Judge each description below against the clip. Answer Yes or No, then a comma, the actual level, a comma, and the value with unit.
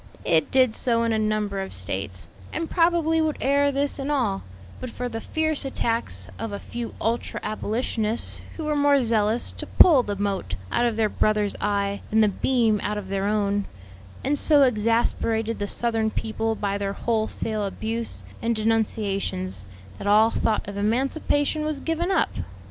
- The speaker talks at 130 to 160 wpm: No, average, 170 wpm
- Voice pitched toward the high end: Yes, high, 225 Hz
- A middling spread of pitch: Yes, average, 4.3 semitones